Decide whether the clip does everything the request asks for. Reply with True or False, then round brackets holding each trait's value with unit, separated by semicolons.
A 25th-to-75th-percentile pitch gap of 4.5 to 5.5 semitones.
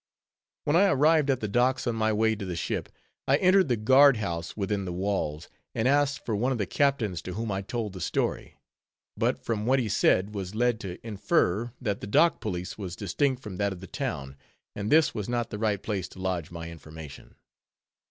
True (5.2 semitones)